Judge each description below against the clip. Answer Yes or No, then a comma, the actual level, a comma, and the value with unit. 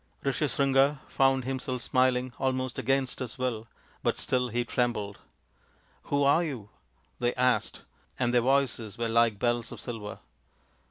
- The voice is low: Yes, low, 125 Hz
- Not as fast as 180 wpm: Yes, average, 150 wpm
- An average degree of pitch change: No, narrow, 2.1 semitones